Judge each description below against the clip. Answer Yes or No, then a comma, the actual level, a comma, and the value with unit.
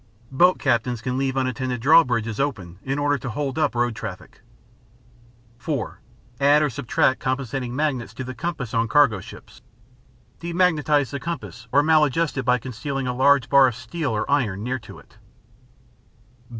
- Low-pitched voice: Yes, low, 130 Hz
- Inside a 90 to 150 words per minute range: No, average, 165 wpm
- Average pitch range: Yes, average, 3.2 semitones